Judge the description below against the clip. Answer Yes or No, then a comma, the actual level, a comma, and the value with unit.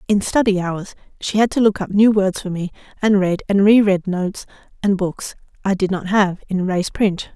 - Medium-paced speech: No, fast, 210 wpm